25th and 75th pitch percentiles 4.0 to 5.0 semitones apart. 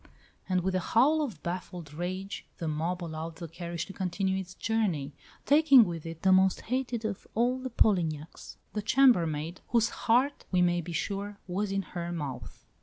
Yes: average, 4.6 semitones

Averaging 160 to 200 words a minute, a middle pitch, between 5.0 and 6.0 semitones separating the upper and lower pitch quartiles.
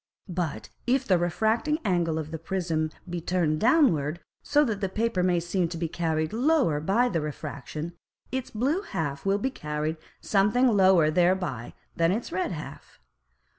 Yes: average, 165 wpm; medium, 175 Hz; wide, 5.6 semitones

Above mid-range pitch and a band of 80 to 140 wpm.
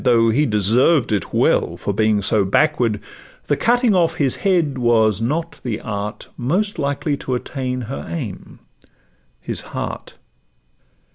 No: low, 125 Hz; slow, 135 wpm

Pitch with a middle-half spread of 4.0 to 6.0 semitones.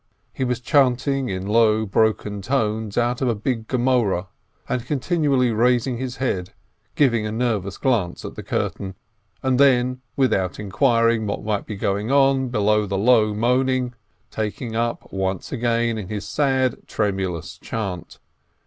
No: average, 3.6 semitones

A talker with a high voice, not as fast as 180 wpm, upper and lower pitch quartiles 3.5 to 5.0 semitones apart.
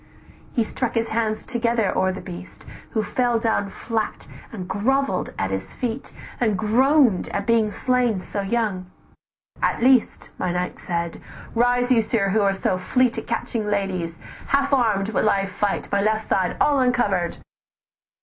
Yes: high, 215 Hz; average, 160 wpm; average, 3.8 semitones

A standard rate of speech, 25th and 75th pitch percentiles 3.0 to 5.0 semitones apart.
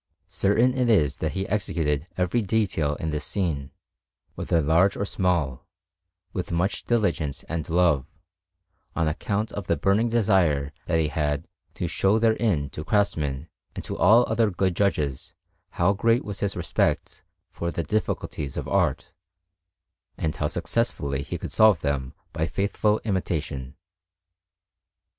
No: average, 145 wpm; wide, 5.5 semitones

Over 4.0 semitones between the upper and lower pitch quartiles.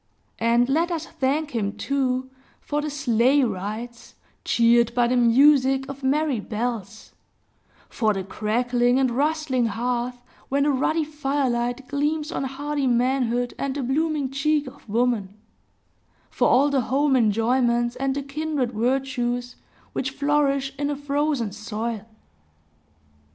No: average, 3.1 semitones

